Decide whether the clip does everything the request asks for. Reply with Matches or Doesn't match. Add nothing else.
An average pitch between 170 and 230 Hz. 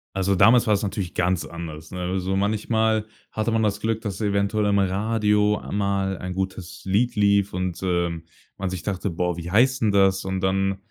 Doesn't match